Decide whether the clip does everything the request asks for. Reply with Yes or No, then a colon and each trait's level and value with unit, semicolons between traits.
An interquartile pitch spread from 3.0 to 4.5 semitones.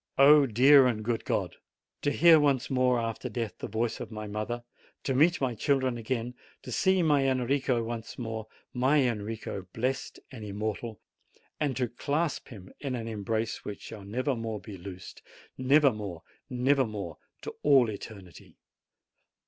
Yes: average, 3.6 semitones